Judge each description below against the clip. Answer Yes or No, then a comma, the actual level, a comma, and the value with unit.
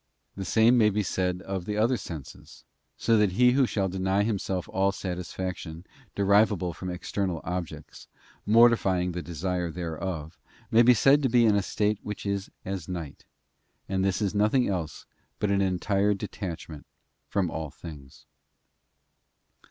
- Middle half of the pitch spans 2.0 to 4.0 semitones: Yes, average, 2.9 semitones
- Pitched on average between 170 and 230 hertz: No, very low, 95 Hz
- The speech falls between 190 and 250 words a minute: No, average, 155 wpm